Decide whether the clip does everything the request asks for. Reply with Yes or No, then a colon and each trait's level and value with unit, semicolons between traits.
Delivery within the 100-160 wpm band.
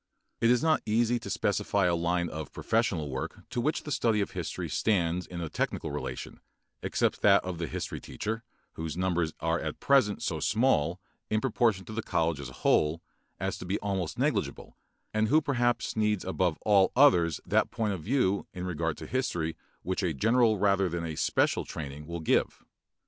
No: average, 190 wpm